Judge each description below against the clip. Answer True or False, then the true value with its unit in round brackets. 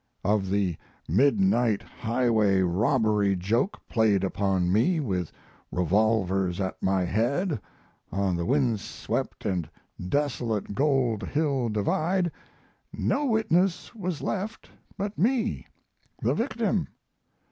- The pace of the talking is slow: True (105 wpm)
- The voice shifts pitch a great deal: True (7.7 semitones)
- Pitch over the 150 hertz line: False (110 Hz)